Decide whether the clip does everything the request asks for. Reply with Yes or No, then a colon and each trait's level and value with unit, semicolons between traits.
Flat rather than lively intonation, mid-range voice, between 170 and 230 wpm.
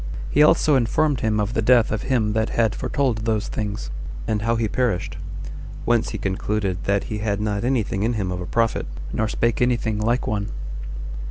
No: narrow, 2.3 semitones; low, 110 Hz; average, 200 wpm